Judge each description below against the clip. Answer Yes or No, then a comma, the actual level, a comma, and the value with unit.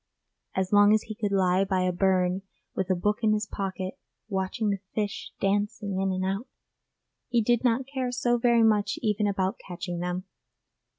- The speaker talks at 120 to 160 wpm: No, average, 180 wpm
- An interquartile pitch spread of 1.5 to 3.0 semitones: Yes, narrow, 2.5 semitones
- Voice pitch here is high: Yes, high, 200 Hz